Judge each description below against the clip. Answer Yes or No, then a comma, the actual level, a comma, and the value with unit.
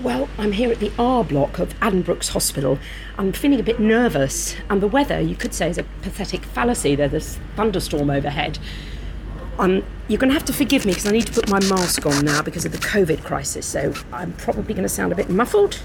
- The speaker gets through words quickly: Yes, fast, 225 wpm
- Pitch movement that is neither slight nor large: No, wide, 7.6 semitones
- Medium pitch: No, high, 195 Hz